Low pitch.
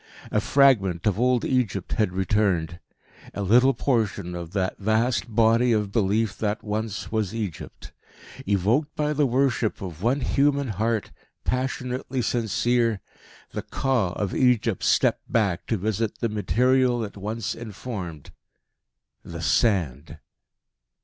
Yes: low, 110 Hz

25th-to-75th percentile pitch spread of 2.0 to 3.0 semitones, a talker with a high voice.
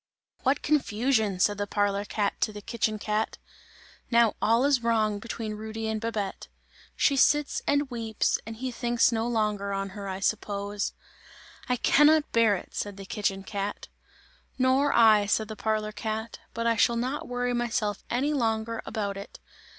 Yes: narrow, 2.6 semitones; high, 220 Hz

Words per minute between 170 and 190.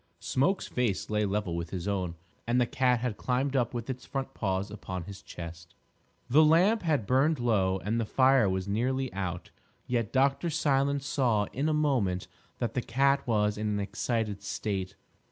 Yes: average, 180 wpm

